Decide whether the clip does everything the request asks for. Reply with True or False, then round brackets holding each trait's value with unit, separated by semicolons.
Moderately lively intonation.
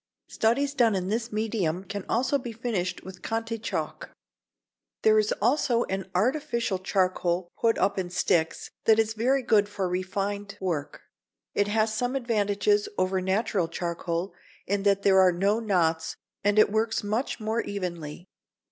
True (3.5 semitones)